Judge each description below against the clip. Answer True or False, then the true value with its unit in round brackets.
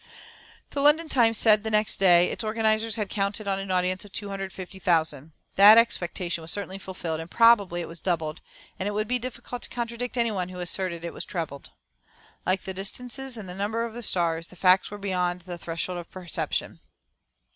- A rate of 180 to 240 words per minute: True (195 wpm)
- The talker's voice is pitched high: True (195 Hz)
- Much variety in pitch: False (3.9 semitones)